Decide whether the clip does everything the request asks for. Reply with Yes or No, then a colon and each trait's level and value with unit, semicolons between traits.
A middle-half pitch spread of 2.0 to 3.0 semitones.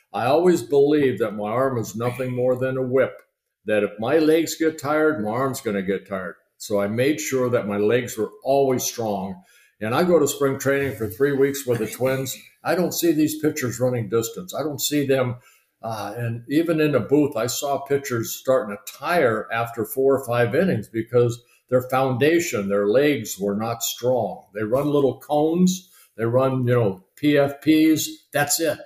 No: average, 4.1 semitones